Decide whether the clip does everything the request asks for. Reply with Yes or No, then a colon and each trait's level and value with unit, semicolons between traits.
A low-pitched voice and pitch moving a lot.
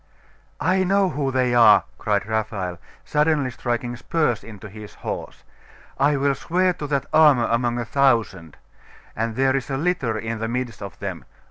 No: low, 125 Hz; average, 4.5 semitones